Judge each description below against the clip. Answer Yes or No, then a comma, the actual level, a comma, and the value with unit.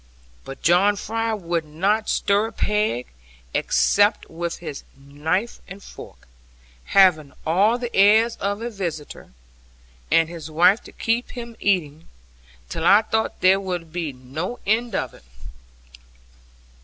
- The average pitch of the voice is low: No, high, 190 Hz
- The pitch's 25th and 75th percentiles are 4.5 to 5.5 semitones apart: Yes, average, 4.8 semitones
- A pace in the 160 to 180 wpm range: No, slow, 135 wpm